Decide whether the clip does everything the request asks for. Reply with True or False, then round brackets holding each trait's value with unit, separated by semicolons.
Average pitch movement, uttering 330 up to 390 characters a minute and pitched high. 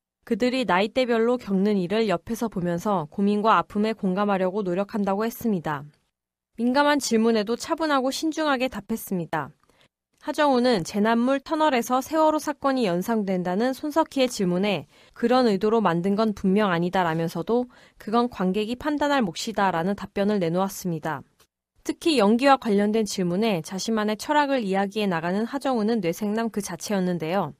True (4.7 semitones; 360 characters per minute; 215 Hz)